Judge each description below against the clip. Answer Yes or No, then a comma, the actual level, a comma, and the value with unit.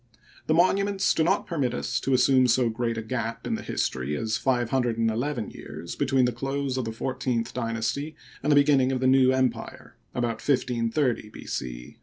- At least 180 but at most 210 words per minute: Yes, average, 200 wpm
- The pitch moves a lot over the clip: No, average, 2.8 semitones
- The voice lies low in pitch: Yes, low, 125 Hz